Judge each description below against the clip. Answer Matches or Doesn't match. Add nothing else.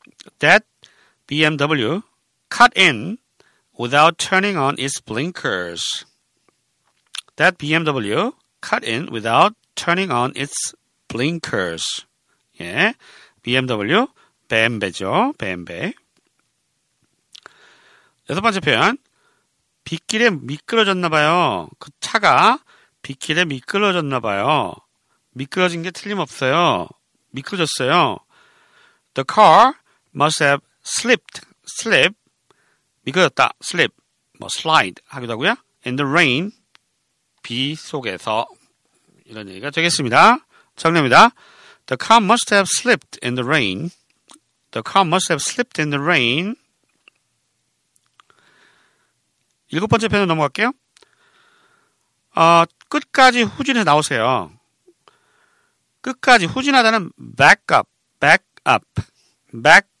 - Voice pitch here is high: Doesn't match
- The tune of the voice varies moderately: Doesn't match